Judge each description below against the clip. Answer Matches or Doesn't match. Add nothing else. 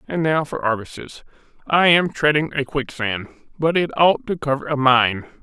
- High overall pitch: Doesn't match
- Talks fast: Doesn't match